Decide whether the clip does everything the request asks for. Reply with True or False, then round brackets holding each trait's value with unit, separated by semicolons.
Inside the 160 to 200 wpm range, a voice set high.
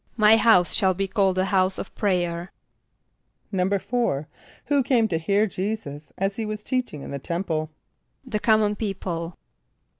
False (150 wpm; 195 Hz)